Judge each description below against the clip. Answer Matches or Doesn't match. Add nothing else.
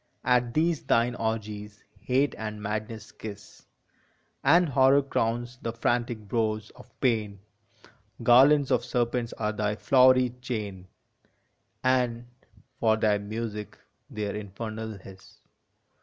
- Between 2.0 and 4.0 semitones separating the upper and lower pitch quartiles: Matches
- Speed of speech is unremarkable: Doesn't match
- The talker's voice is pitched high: Doesn't match